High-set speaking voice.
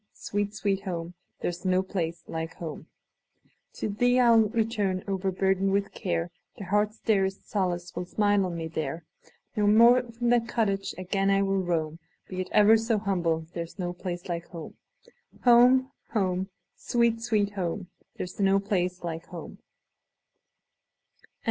Yes: high, 195 Hz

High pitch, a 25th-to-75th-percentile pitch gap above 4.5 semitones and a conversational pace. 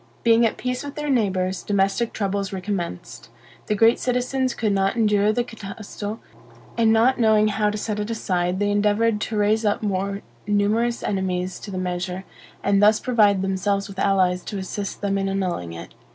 No: high, 205 Hz; narrow, 2.5 semitones; average, 180 wpm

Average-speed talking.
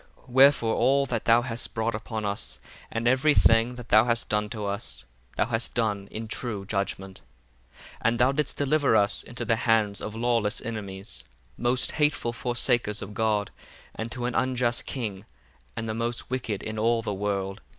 Yes: average, 180 wpm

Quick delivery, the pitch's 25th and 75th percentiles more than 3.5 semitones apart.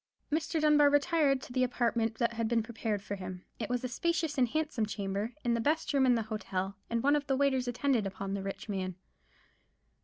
Yes: fast, 210 wpm; average, 4.9 semitones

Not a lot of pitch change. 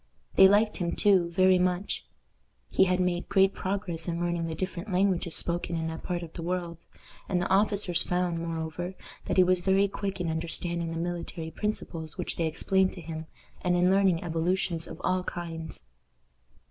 Yes: narrow, 2.1 semitones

